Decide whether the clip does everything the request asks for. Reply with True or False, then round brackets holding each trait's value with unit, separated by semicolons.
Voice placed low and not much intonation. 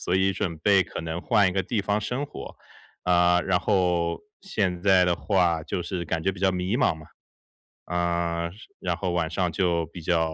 True (90 Hz; 2.2 semitones)